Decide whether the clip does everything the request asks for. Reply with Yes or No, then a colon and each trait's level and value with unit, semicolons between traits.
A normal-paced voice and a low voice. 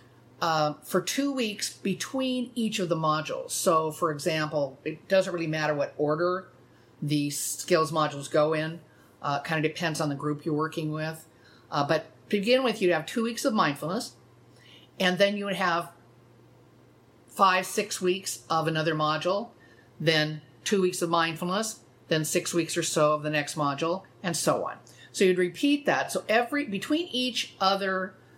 No: average, 170 wpm; medium, 165 Hz